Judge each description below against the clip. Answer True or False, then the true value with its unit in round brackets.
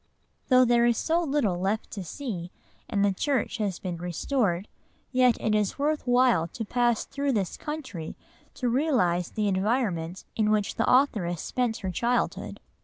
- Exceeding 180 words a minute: False (170 wpm)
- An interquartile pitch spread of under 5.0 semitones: False (5.3 semitones)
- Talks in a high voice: True (220 Hz)